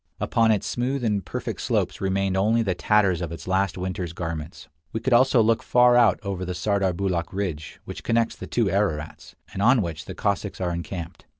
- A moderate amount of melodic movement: Yes, average, 4.1 semitones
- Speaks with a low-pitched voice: Yes, low, 100 Hz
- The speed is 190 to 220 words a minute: Yes, average, 195 wpm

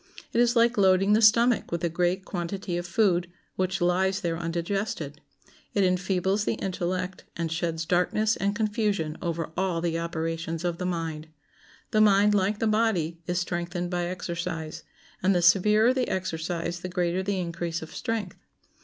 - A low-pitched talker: No, medium, 180 Hz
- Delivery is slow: No, average, 165 wpm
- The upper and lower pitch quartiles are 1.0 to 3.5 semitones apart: Yes, average, 2.8 semitones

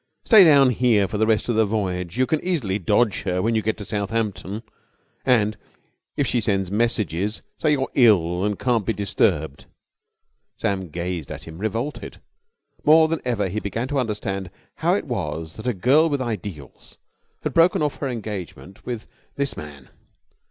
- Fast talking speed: No, average, 175 wpm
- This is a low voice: Yes, low, 105 Hz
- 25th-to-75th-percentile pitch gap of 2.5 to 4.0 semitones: No, average, 4.9 semitones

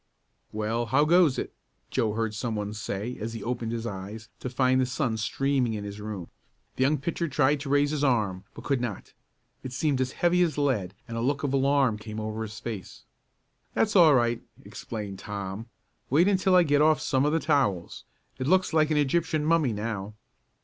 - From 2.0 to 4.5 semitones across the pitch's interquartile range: No, average, 5.3 semitones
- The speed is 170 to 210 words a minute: Yes, average, 200 wpm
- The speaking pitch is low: Yes, low, 125 Hz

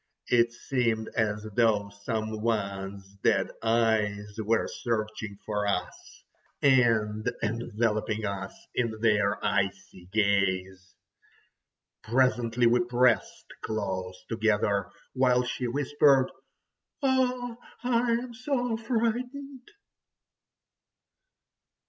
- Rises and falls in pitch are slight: No, average, 3.9 semitones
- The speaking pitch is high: No, low, 110 Hz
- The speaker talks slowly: Yes, slow, 90 wpm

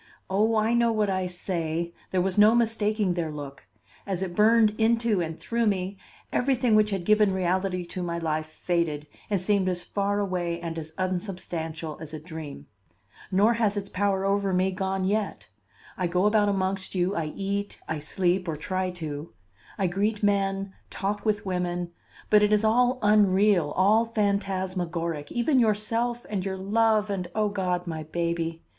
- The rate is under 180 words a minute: Yes, average, 170 wpm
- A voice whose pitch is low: No, high, 190 Hz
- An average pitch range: Yes, average, 3.2 semitones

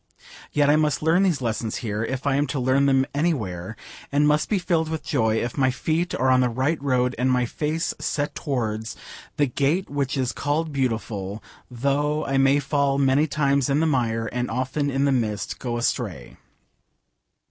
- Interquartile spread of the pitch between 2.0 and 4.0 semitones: Yes, average, 3.3 semitones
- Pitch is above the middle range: No, low, 135 Hz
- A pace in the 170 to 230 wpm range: Yes, average, 190 wpm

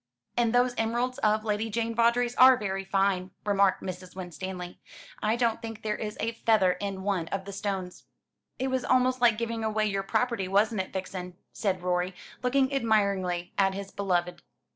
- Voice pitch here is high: Yes, high, 210 Hz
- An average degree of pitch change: Yes, average, 3.4 semitones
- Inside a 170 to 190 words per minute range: Yes, average, 175 wpm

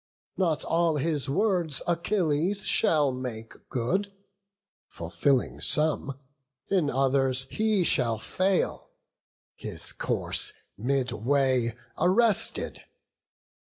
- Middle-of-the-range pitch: Yes, medium, 145 Hz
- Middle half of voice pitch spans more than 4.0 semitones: Yes, wide, 5.6 semitones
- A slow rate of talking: Yes, slow, 85 wpm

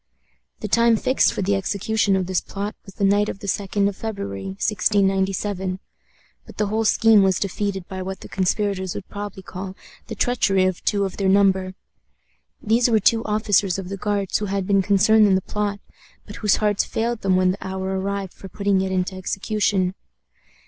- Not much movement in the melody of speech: Yes, narrow, 1.7 semitones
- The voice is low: No, high, 195 Hz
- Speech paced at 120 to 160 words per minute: No, average, 190 wpm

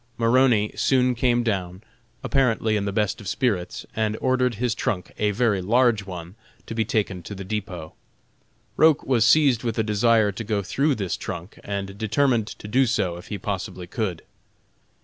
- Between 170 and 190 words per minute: Yes, average, 175 wpm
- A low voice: Yes, low, 110 Hz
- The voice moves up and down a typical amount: Yes, average, 3.8 semitones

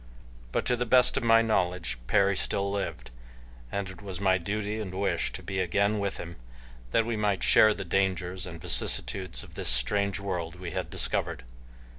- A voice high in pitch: No, low, 100 Hz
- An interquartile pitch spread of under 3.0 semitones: Yes, narrow, 2.4 semitones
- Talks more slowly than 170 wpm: No, average, 185 wpm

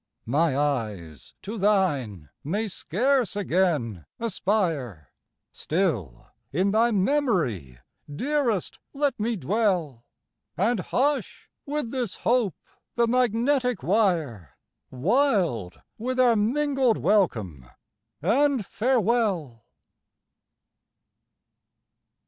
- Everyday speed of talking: No, slow, 85 wpm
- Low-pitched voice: No, high, 195 Hz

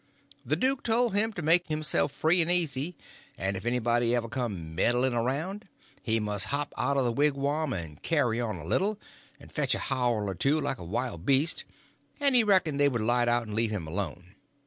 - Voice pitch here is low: Yes, low, 130 Hz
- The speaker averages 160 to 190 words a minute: No, fast, 205 wpm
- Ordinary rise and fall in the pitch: No, wide, 6.0 semitones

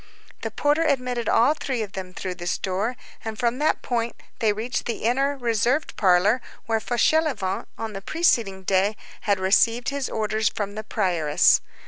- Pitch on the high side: Yes, high, 225 Hz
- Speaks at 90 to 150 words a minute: No, average, 165 wpm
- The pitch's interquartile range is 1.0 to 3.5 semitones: No, average, 4.2 semitones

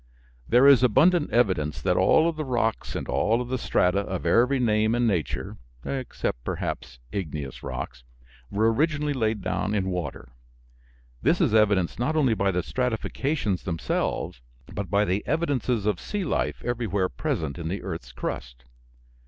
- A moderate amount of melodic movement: No, wide, 5.9 semitones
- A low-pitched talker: Yes, low, 110 Hz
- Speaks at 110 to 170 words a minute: Yes, average, 160 wpm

